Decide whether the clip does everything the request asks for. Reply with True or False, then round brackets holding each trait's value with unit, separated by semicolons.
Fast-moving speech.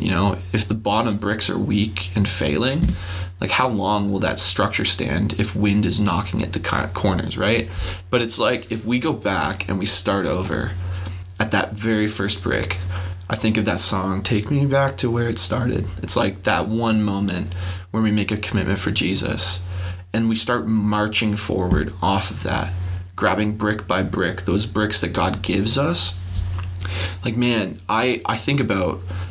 False (180 wpm)